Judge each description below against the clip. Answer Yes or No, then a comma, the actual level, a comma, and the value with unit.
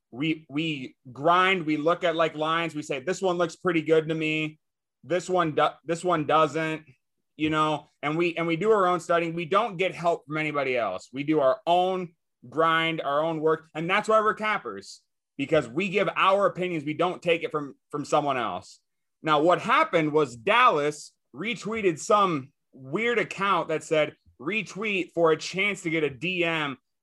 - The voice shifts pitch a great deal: No, narrow, 2.6 semitones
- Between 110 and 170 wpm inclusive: No, average, 190 wpm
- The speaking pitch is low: No, medium, 165 Hz